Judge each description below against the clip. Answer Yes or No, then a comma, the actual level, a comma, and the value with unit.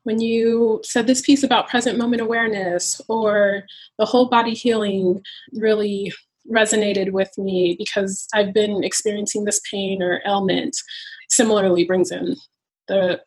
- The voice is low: No, high, 210 Hz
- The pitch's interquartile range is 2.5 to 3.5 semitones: Yes, average, 2.9 semitones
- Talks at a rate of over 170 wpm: No, slow, 135 wpm